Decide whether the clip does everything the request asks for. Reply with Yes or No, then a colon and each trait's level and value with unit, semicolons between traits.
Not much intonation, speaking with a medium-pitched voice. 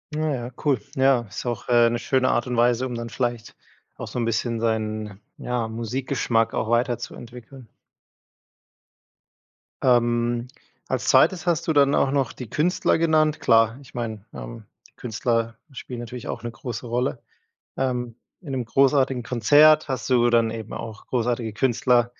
No: narrow, 2.3 semitones; low, 120 Hz